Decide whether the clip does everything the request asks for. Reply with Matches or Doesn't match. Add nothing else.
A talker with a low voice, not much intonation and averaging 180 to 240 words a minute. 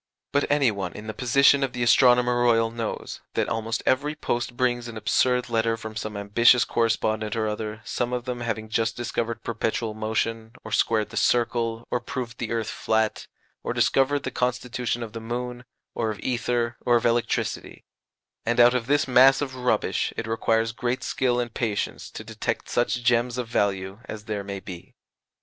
Matches